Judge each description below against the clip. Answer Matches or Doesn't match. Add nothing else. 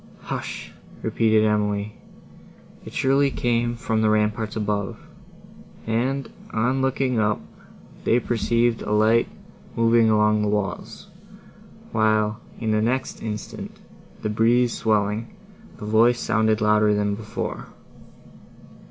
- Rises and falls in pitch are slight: Matches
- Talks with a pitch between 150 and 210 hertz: Doesn't match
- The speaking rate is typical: Doesn't match